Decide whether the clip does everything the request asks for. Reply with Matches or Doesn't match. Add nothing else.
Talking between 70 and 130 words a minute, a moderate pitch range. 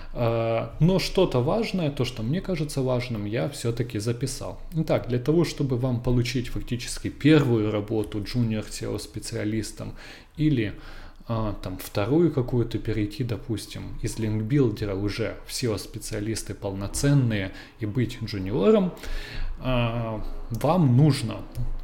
Matches